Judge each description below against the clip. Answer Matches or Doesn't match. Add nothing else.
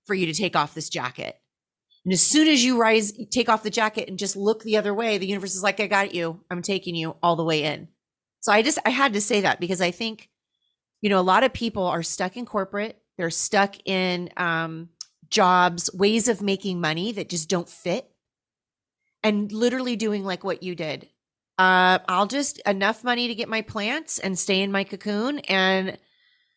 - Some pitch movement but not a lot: Matches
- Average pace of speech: Doesn't match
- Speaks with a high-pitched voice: Matches